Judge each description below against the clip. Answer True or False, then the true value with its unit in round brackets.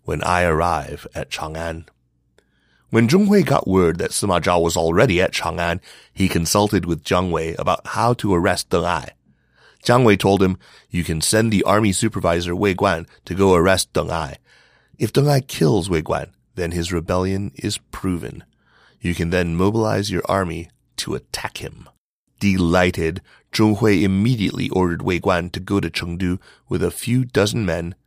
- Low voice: True (95 Hz)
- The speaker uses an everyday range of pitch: True (3.2 semitones)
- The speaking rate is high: False (170 wpm)